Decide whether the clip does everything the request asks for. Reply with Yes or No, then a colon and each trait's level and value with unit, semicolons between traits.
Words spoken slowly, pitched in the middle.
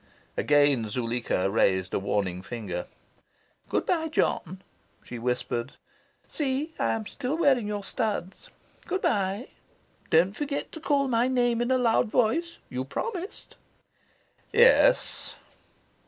No: slow, 125 wpm; high, 215 Hz